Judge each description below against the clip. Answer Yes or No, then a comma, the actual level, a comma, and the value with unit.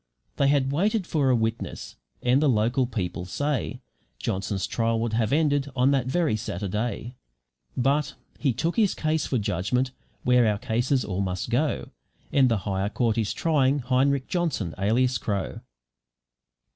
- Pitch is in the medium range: No, low, 125 Hz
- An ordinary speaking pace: Yes, average, 155 wpm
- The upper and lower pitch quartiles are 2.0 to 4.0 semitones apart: No, average, 4.6 semitones